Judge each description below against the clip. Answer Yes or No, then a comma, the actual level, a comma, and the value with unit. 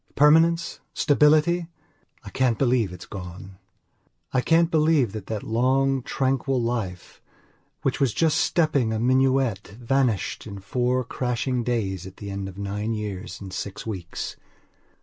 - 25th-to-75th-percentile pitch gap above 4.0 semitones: Yes, average, 5.1 semitones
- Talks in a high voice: No, low, 120 Hz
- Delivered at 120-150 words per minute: Yes, average, 140 wpm